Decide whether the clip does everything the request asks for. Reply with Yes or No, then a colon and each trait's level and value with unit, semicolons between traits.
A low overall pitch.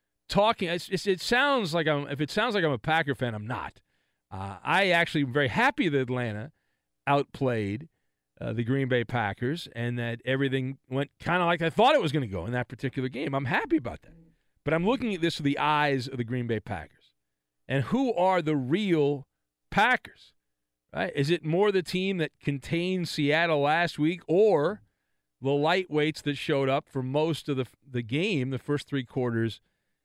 No: medium, 145 Hz